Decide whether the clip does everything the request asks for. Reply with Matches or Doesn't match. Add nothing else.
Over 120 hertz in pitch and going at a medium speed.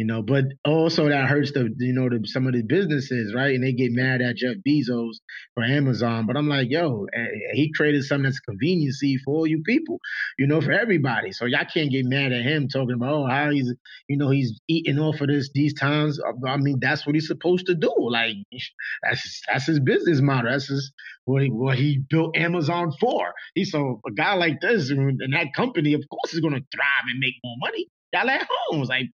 Doesn't match